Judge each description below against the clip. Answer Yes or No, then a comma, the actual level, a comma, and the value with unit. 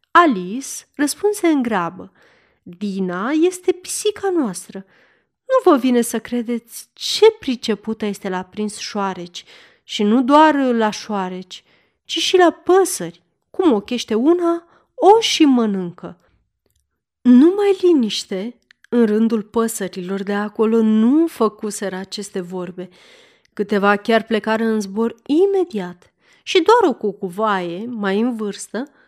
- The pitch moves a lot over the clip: Yes, wide, 8.1 semitones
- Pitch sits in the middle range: No, high, 225 Hz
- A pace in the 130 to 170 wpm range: No, average, 120 wpm